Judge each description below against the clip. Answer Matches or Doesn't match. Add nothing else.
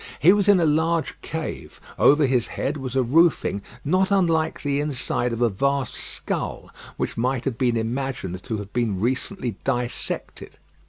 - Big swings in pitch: Doesn't match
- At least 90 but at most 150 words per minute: Doesn't match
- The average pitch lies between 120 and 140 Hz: Matches